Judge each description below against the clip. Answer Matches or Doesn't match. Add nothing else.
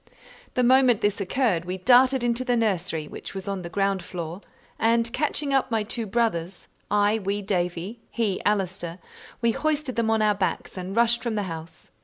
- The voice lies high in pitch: Matches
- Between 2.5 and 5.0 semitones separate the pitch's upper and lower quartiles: Matches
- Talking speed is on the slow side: Doesn't match